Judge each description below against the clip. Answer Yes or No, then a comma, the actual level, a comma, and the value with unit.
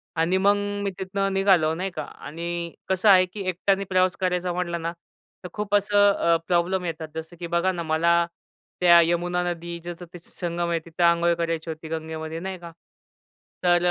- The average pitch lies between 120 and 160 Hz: No, medium, 175 Hz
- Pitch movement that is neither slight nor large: No, narrow, 1.8 semitones